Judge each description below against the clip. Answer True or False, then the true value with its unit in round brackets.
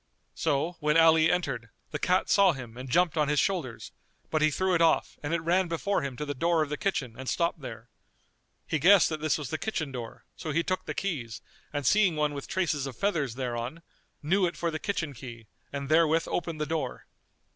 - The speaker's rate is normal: False (220 wpm)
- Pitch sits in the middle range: True (155 Hz)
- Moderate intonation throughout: True (3.8 semitones)